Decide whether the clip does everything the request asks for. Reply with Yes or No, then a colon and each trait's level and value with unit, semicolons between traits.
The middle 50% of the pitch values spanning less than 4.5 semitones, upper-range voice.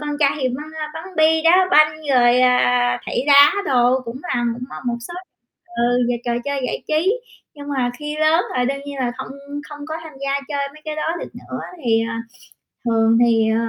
Yes: average, 3.8 semitones; very high, 275 Hz